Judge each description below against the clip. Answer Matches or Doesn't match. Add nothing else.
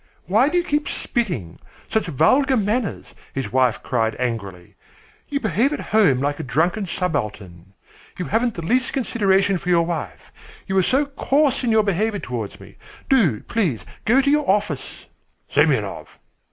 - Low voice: Doesn't match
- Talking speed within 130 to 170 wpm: Matches